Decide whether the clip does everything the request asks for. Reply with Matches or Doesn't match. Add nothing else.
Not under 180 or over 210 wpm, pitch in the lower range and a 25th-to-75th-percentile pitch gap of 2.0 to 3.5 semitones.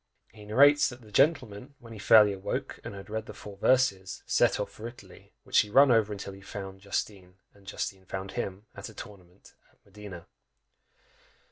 Matches